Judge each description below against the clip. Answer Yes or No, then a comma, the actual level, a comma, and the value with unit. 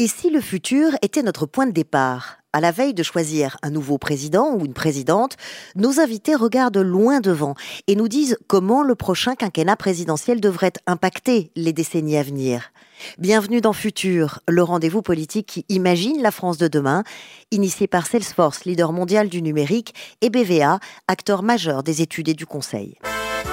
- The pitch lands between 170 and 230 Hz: Yes, medium, 185 Hz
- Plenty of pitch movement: Yes, wide, 5.8 semitones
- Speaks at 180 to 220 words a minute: No, average, 170 wpm